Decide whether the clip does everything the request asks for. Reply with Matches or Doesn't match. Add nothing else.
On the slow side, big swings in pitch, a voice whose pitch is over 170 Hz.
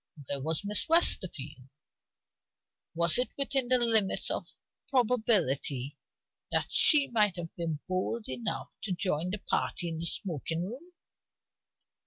Matches